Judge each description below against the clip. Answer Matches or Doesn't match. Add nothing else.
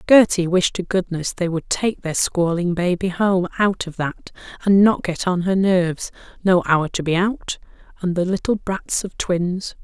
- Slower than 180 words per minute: Doesn't match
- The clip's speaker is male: Doesn't match